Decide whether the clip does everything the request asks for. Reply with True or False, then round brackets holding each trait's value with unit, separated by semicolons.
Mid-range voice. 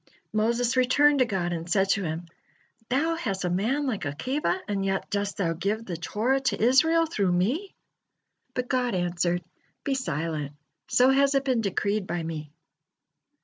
False (210 Hz)